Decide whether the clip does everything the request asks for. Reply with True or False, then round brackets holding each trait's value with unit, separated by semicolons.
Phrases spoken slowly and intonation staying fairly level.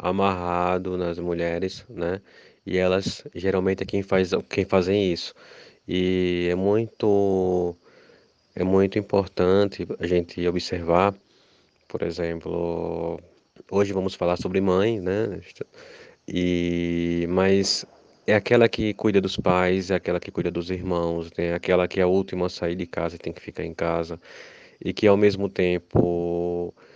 False (145 wpm; 2.1 semitones)